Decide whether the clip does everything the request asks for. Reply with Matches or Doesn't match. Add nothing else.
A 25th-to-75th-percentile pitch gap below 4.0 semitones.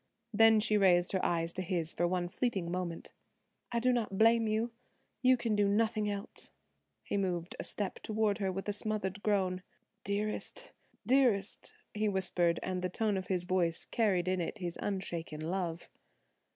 Matches